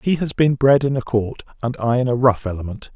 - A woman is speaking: No, male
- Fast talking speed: Yes, fast, 265 wpm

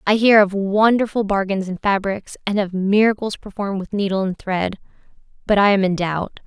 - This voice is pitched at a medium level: No, high, 200 Hz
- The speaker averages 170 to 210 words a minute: Yes, average, 185 wpm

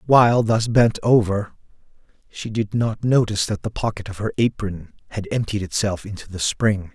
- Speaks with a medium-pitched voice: No, low, 105 Hz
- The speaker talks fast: No, average, 175 wpm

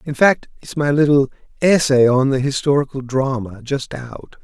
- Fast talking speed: No, average, 160 wpm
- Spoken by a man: Yes, male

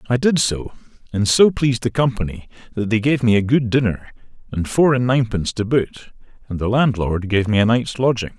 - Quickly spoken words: Yes, fast, 210 wpm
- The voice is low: Yes, low, 115 Hz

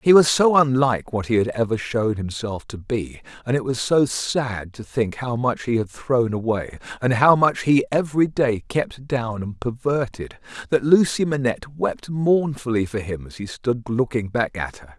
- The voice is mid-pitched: No, low, 120 Hz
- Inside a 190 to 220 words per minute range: Yes, average, 195 wpm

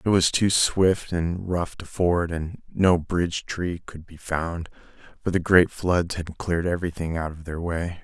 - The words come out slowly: No, average, 195 wpm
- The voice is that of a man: Yes, male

